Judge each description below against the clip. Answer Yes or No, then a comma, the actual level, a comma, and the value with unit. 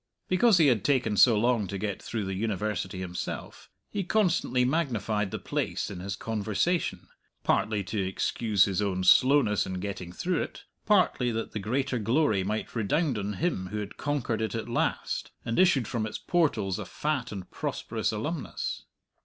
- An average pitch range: No, wide, 5.7 semitones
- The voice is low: Yes, low, 110 Hz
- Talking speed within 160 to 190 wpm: Yes, average, 170 wpm